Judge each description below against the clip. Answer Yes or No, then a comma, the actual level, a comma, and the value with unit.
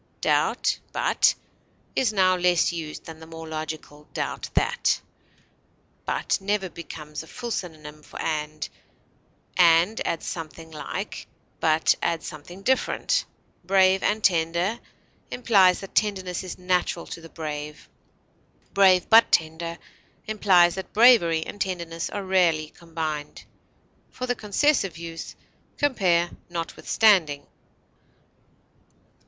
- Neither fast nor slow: No, slow, 115 wpm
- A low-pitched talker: No, medium, 175 Hz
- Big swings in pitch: No, average, 3.3 semitones